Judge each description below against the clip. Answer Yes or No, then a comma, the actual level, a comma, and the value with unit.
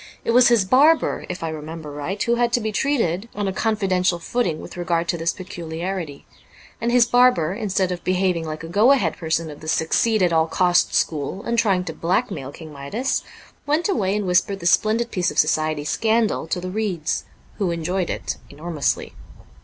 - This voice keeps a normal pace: Yes, average, 195 wpm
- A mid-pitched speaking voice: Yes, medium, 180 Hz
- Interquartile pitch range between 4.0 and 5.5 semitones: Yes, average, 5.1 semitones